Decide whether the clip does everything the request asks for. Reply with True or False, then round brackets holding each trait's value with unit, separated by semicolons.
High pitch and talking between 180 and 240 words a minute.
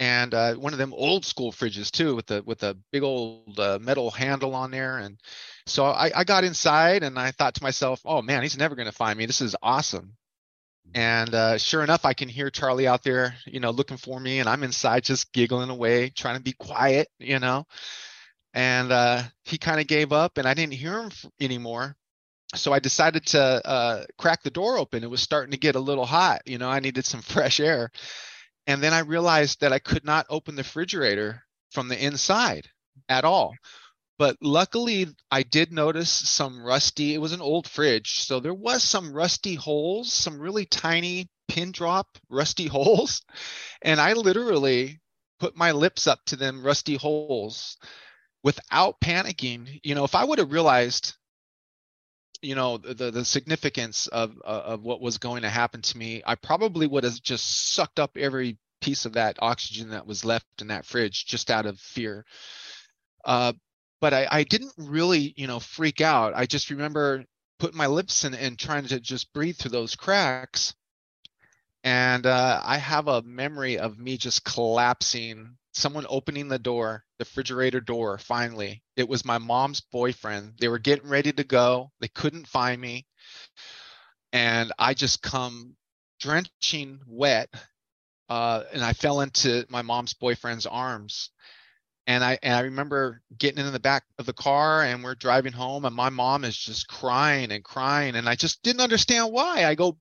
False (130 Hz; 185 wpm)